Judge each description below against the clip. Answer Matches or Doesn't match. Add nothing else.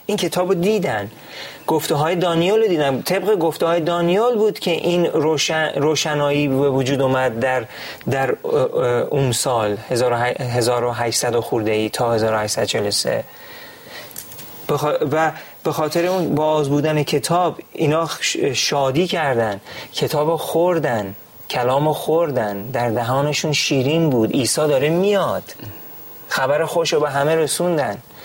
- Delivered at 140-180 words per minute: Doesn't match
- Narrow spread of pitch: Doesn't match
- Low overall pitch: Doesn't match